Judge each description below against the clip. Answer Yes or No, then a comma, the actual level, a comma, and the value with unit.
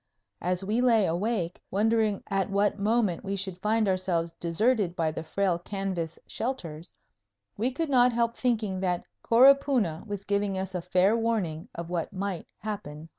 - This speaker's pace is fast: No, average, 170 wpm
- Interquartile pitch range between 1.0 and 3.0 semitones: No, average, 4.2 semitones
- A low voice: No, high, 195 Hz